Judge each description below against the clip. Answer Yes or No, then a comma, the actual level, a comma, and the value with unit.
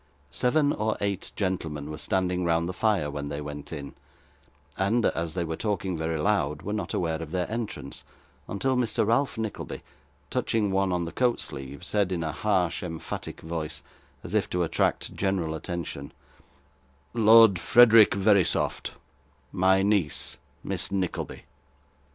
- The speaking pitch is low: Yes, very low, 90 Hz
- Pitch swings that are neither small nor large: Yes, average, 4.6 semitones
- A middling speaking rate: Yes, average, 150 wpm